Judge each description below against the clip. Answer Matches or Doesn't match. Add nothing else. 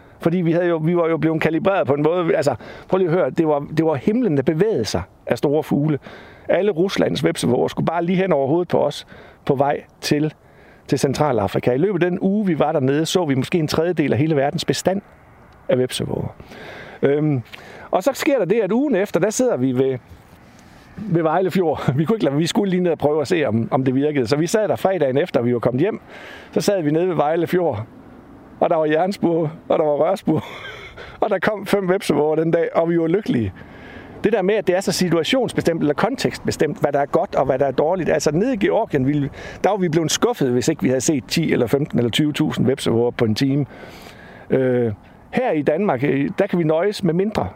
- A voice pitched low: Doesn't match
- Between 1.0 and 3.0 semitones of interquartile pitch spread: Doesn't match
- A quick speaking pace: Matches